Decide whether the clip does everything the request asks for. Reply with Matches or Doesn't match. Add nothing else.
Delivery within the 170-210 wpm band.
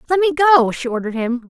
Doesn't match